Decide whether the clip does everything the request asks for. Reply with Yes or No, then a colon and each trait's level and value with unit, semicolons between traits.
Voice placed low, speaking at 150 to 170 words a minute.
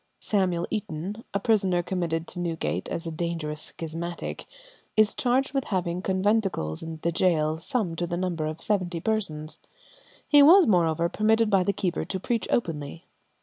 No: medium, 175 Hz; average, 160 wpm